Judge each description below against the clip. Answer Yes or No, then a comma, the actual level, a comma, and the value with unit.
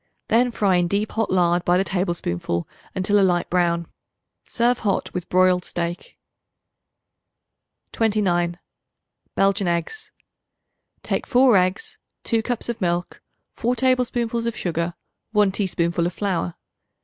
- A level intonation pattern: No, average, 4.4 semitones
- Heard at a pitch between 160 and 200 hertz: Yes, high, 190 Hz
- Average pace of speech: No, slow, 125 wpm